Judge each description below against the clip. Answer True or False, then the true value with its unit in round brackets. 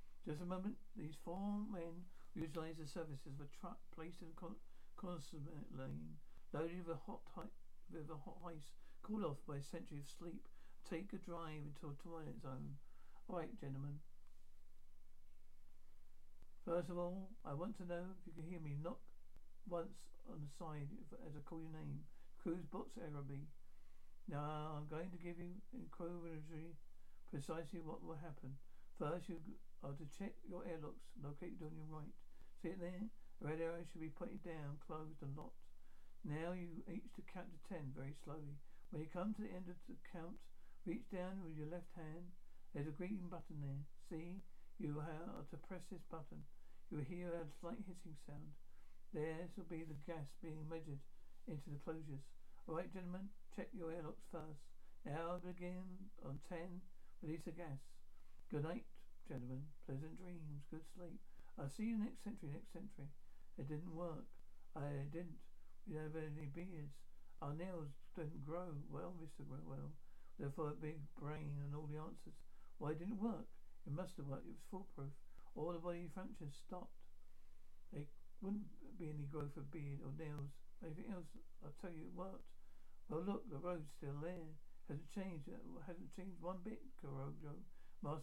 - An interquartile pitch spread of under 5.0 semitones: True (3.9 semitones)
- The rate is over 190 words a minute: False (175 wpm)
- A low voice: False (155 Hz)